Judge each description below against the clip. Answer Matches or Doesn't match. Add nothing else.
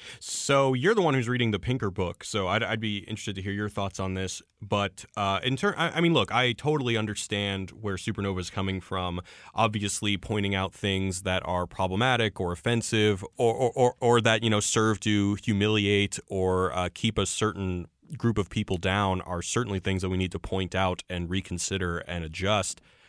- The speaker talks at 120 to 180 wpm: Doesn't match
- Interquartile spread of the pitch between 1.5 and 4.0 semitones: Matches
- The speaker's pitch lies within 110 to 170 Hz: Doesn't match